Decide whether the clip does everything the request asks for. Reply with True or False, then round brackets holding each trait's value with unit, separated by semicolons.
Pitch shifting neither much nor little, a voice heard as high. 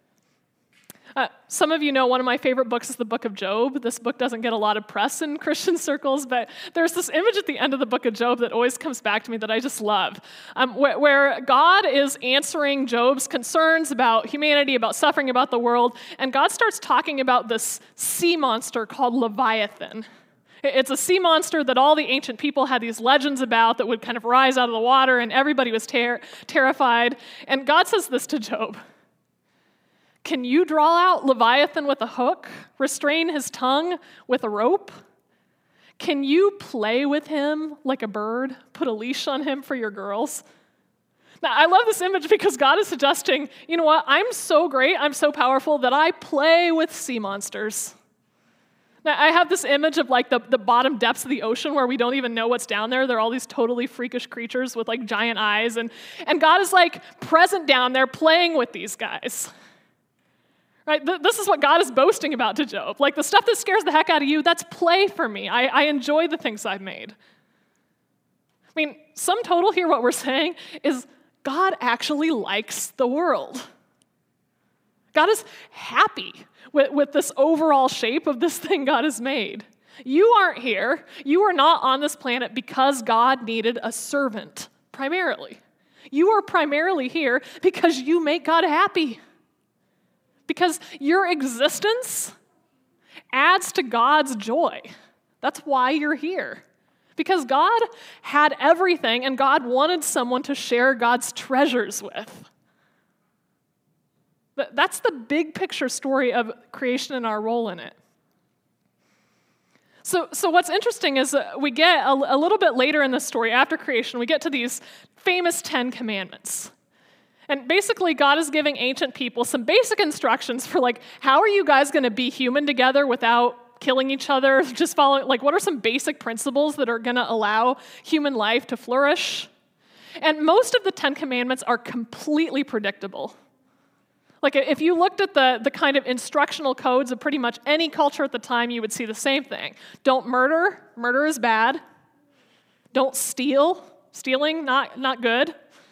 True (4.3 semitones; 275 Hz)